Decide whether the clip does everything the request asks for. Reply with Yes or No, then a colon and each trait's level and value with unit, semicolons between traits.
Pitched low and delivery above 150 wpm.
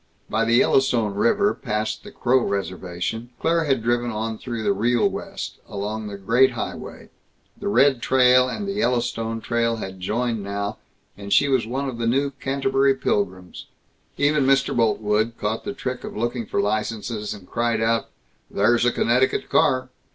Yes: low, 115 Hz; average, 165 wpm